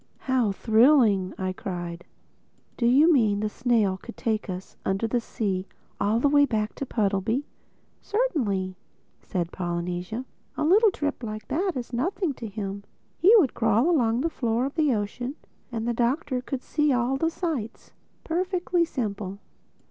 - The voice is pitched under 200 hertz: No, high, 235 Hz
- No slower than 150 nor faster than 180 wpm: Yes, average, 155 wpm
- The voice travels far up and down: Yes, wide, 6.0 semitones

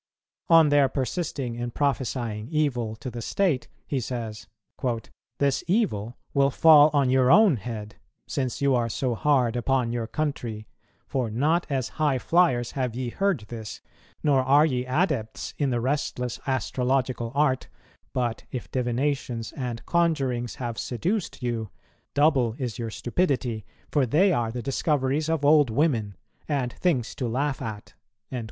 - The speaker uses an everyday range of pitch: Yes, average, 3.7 semitones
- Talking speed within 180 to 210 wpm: No, average, 145 wpm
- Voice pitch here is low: Yes, low, 130 Hz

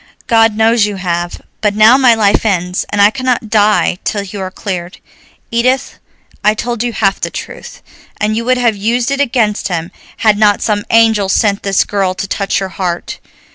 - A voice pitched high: Yes, high, 210 Hz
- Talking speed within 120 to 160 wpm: No, average, 190 wpm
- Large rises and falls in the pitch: No, average, 2.7 semitones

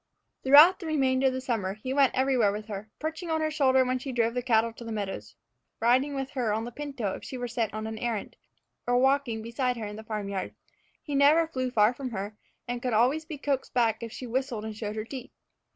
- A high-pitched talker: Yes, high, 245 Hz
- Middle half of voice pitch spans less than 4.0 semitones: Yes, average, 3.6 semitones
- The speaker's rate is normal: No, fast, 240 wpm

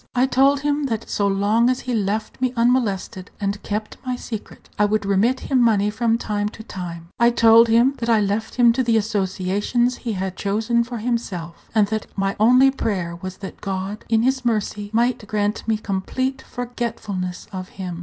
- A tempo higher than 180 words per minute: Yes, average, 190 wpm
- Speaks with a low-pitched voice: No, high, 220 Hz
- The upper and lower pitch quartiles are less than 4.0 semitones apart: Yes, average, 3.3 semitones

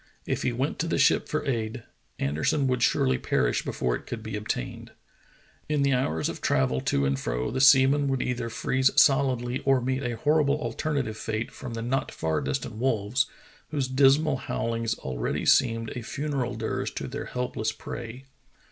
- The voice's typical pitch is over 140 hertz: No, low, 125 Hz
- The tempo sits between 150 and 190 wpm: Yes, average, 180 wpm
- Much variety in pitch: No, average, 3.8 semitones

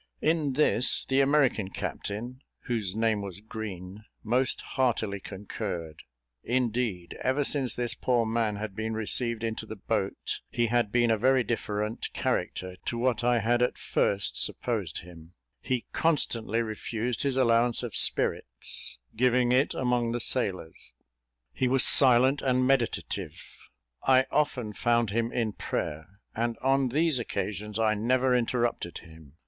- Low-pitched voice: Yes, low, 115 Hz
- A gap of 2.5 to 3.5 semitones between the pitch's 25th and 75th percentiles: Yes, average, 3.2 semitones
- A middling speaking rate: Yes, average, 145 wpm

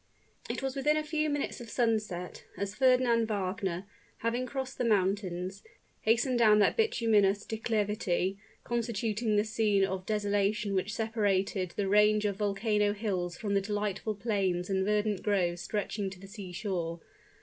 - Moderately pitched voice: No, high, 210 Hz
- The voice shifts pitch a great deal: No, narrow, 2.6 semitones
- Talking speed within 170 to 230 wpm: No, average, 150 wpm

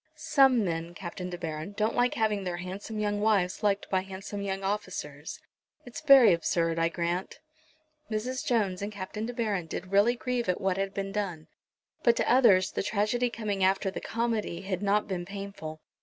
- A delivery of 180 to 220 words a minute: Yes, average, 185 wpm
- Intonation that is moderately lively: Yes, average, 3.2 semitones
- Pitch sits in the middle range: No, high, 200 Hz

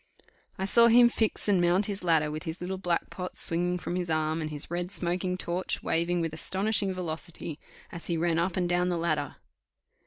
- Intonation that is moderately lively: No, narrow, 2.0 semitones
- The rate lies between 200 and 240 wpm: Yes, fast, 205 wpm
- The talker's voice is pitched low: No, medium, 175 Hz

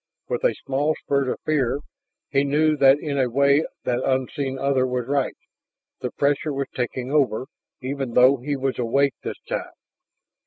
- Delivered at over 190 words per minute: No, average, 165 wpm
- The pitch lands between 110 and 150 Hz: Yes, low, 135 Hz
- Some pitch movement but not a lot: No, narrow, 1.7 semitones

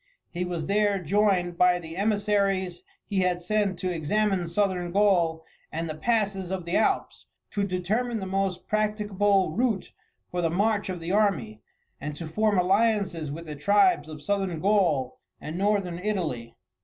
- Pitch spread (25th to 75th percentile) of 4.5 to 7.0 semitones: No, average, 3.3 semitones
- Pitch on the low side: No, high, 190 Hz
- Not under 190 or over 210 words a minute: No, average, 160 wpm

